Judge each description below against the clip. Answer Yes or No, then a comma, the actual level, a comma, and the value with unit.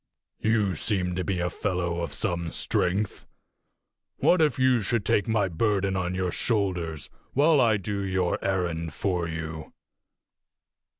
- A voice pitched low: Yes, very low, 95 Hz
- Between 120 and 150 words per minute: Yes, average, 140 wpm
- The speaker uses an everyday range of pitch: Yes, average, 3.4 semitones